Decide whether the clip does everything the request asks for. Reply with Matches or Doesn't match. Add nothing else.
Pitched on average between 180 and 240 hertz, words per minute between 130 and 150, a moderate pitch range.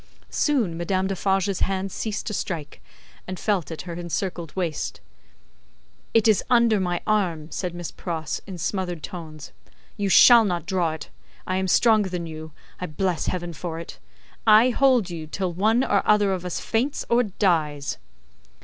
Doesn't match